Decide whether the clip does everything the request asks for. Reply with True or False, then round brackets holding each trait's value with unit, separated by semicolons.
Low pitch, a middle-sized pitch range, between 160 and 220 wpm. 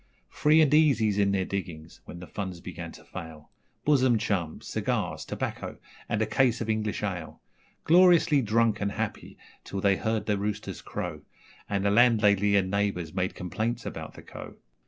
True (100 Hz; 3.7 semitones; 170 wpm)